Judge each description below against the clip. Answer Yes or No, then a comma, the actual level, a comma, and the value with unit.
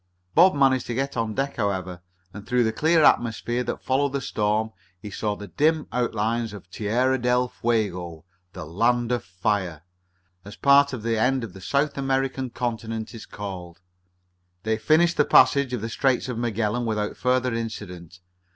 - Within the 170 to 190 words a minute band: Yes, average, 175 wpm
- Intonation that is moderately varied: Yes, average, 4.0 semitones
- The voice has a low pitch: Yes, low, 115 Hz